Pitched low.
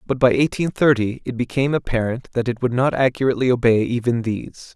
Yes: low, 125 Hz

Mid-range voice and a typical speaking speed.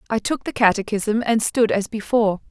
No: high, 220 Hz; average, 190 wpm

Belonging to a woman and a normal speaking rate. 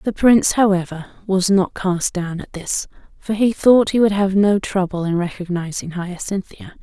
Yes: female; average, 175 wpm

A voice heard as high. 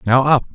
No: low, 130 Hz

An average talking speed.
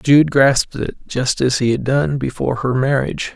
Yes: average, 180 wpm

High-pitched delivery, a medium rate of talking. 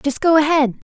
Yes: very high, 290 Hz; average, 190 wpm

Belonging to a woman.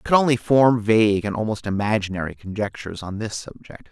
No: male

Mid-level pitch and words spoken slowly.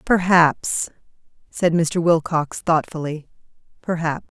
Yes: medium, 165 Hz; slow, 70 wpm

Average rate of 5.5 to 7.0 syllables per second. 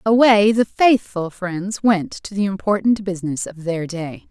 No: 4.3 syllables/s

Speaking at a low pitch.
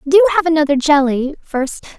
No: very high, 305 Hz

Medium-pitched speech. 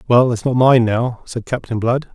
No: low, 120 Hz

